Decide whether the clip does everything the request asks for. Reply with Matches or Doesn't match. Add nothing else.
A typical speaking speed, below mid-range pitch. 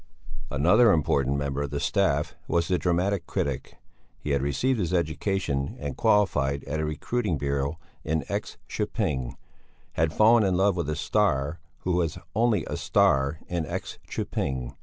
Matches